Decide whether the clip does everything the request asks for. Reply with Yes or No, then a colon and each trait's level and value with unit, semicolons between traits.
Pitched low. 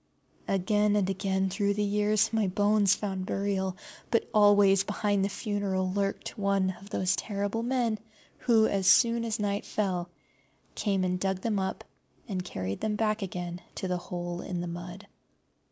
No: high, 200 Hz